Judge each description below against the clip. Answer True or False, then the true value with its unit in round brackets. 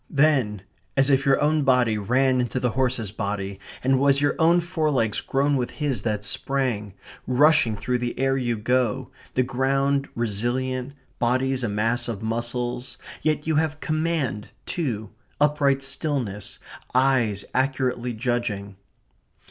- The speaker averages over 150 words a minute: False (140 wpm)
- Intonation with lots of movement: False (3.3 semitones)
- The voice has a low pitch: True (130 Hz)